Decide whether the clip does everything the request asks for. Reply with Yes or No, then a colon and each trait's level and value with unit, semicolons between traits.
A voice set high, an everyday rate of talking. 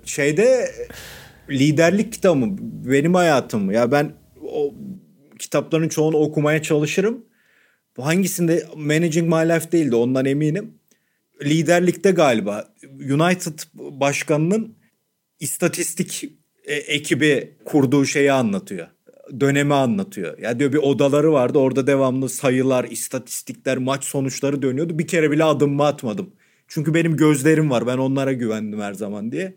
No: medium, 155 Hz; average, 125 wpm